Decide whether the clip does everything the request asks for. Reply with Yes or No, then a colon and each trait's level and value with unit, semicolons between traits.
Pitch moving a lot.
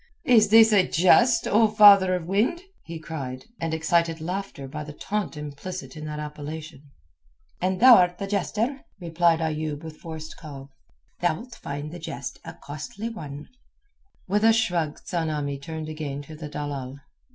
No: average, 4.7 semitones